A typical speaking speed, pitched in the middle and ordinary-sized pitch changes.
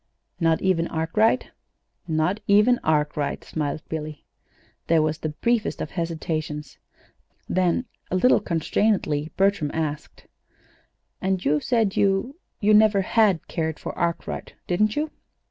No: slow, 125 wpm; medium, 170 Hz; average, 4.9 semitones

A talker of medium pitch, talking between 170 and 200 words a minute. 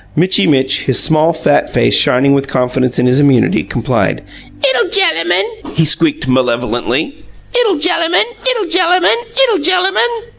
No: medium, 170 Hz; average, 140 wpm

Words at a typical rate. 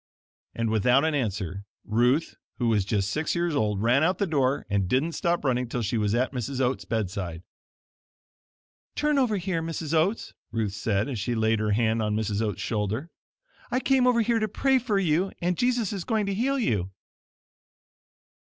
Yes: average, 185 wpm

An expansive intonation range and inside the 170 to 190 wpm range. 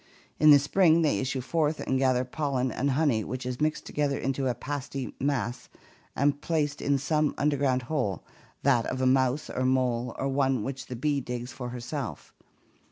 No: narrow, 2.4 semitones; average, 185 wpm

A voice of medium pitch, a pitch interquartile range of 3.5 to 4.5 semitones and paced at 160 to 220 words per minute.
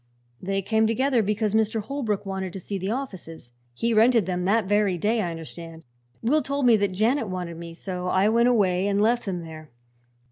No: high, 200 Hz; average, 3.9 semitones; average, 200 wpm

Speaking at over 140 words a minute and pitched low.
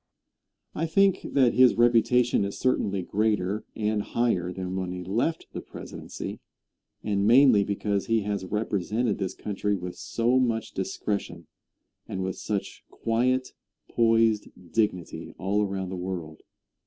No: slow, 135 wpm; low, 105 Hz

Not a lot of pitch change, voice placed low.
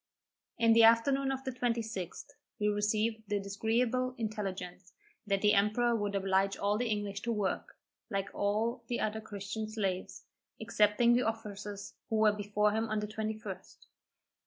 No: narrow, 2.1 semitones; high, 215 Hz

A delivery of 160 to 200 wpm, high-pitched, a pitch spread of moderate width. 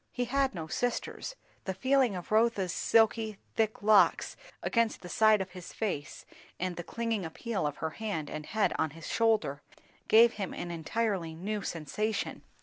Yes: average, 165 wpm; high, 205 Hz; average, 4.7 semitones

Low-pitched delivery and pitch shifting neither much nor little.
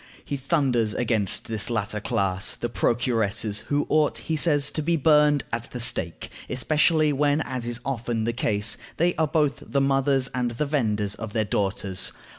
Yes: low, 125 Hz; average, 4.8 semitones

